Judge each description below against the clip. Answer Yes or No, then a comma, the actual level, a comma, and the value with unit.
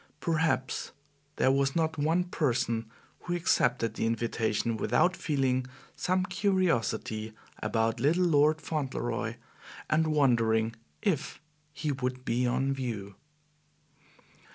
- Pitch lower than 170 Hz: Yes, low, 135 Hz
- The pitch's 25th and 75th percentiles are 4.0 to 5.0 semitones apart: No, wide, 5.6 semitones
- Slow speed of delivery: Yes, slow, 105 wpm